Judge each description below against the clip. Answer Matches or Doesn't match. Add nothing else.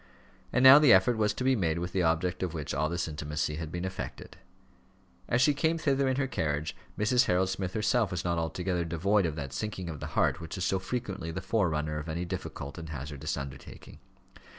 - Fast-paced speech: Matches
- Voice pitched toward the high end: Doesn't match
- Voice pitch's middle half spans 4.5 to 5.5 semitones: Matches